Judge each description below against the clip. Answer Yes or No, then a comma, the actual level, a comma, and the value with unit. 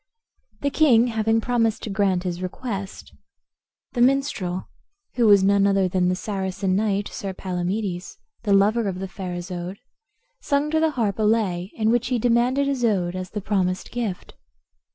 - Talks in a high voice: Yes, high, 200 Hz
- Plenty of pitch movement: No, average, 4.2 semitones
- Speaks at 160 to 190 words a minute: Yes, average, 165 wpm